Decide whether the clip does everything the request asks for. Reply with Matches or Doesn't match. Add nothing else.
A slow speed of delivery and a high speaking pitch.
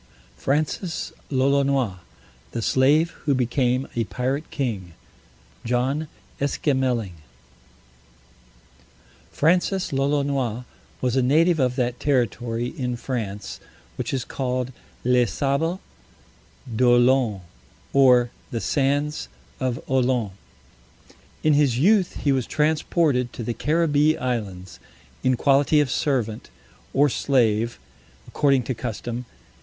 Doesn't match